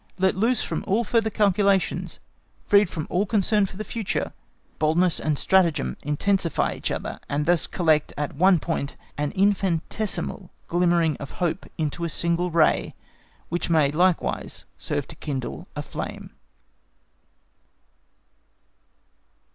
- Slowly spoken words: Yes, slow, 130 wpm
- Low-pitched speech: No, medium, 175 Hz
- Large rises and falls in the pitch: No, average, 3.9 semitones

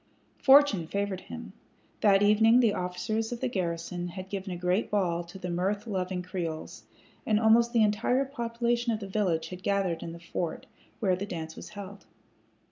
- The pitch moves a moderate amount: Yes, average, 3.6 semitones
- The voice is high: Yes, high, 195 Hz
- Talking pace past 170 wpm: Yes, average, 180 wpm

